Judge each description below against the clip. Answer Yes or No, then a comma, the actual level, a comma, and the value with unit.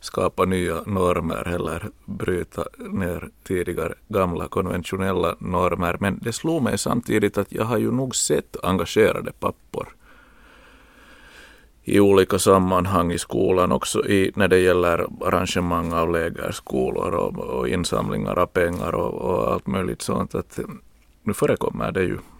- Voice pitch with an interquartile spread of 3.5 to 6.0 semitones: No, average, 2.8 semitones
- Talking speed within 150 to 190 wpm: No, average, 135 wpm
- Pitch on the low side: Yes, very low, 95 Hz